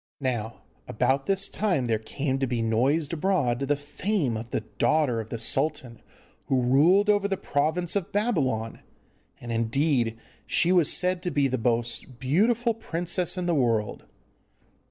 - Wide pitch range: Yes, wide, 7.0 semitones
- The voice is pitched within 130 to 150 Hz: Yes, medium, 140 Hz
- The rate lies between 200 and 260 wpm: No, average, 155 wpm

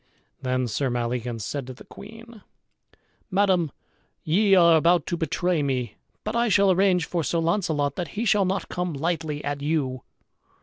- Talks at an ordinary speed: Yes, average, 165 wpm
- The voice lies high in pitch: No, medium, 165 Hz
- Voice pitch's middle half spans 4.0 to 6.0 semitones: Yes, average, 5.3 semitones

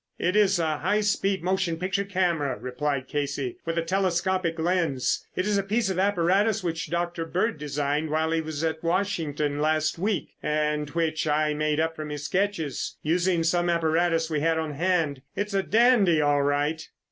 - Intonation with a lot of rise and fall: No, average, 3.6 semitones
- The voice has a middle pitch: Yes, medium, 165 Hz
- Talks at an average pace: Yes, average, 175 wpm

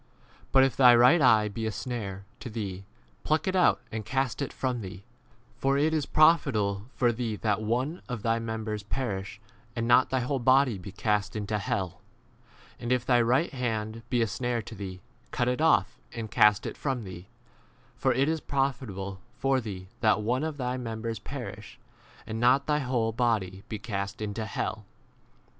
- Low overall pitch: Yes, low, 115 Hz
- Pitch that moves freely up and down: No, average, 3.7 semitones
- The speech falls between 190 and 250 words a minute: Yes, average, 195 wpm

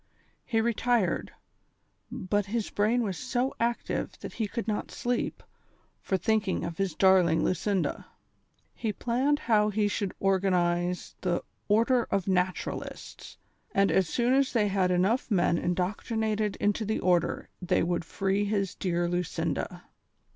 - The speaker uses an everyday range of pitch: Yes, average, 3.6 semitones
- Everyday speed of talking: Yes, average, 145 wpm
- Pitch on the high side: Yes, high, 200 Hz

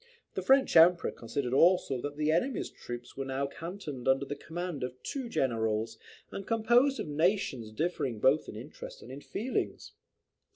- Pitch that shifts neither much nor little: No, wide, 5.8 semitones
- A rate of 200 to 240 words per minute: No, average, 165 wpm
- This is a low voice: No, medium, 145 Hz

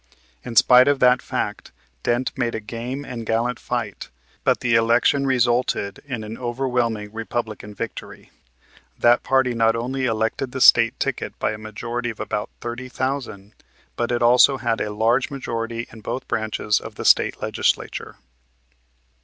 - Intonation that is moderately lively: No, narrow, 2.0 semitones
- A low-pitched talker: Yes, low, 120 Hz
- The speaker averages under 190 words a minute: Yes, average, 155 wpm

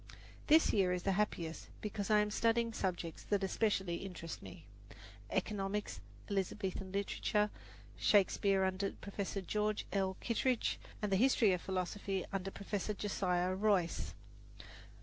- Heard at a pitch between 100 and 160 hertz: No, high, 195 Hz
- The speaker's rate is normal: No, slow, 130 wpm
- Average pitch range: No, narrow, 1.9 semitones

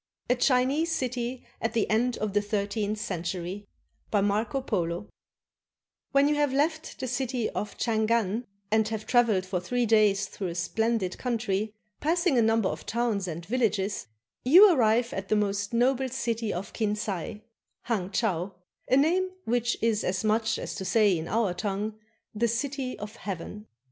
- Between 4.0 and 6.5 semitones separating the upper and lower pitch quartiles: No, average, 3.5 semitones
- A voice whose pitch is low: No, high, 220 Hz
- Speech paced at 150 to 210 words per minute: Yes, average, 165 wpm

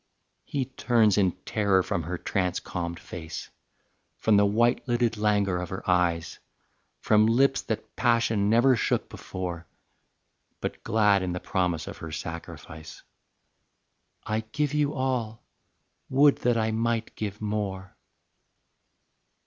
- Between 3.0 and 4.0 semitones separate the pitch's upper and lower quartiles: No, average, 4.5 semitones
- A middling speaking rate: No, slow, 130 wpm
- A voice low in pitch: Yes, low, 105 Hz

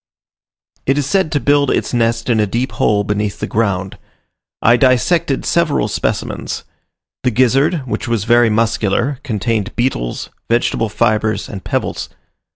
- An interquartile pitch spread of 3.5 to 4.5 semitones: Yes, average, 3.9 semitones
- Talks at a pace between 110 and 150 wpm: Yes, average, 145 wpm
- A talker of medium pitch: No, low, 120 Hz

